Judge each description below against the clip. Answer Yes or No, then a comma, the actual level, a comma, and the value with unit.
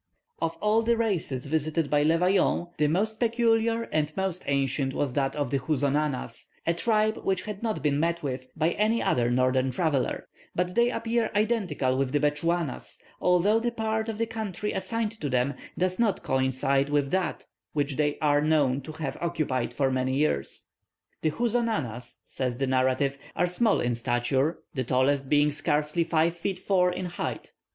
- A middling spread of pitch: No, wide, 6.3 semitones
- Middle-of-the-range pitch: Yes, medium, 155 Hz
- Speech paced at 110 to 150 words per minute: No, average, 175 wpm